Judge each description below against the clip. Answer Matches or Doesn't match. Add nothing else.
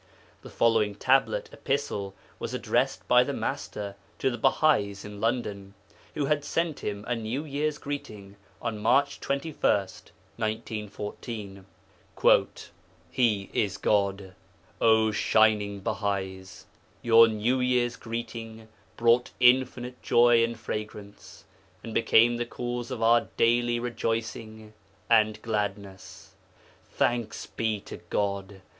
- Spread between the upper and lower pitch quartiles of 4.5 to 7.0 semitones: Doesn't match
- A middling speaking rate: Doesn't match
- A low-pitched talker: Matches